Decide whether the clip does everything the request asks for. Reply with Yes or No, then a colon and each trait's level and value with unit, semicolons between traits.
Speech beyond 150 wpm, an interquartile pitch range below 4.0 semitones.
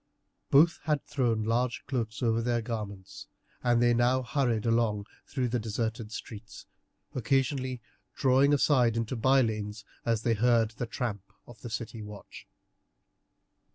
No: average, 140 wpm; narrow, 2.4 semitones